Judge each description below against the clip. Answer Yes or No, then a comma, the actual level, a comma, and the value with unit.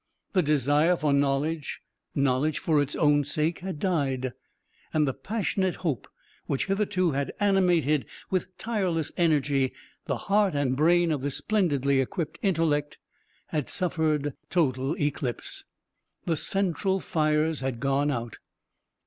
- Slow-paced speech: Yes, slow, 130 wpm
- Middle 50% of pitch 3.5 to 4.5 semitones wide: Yes, average, 4.0 semitones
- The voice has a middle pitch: Yes, medium, 155 Hz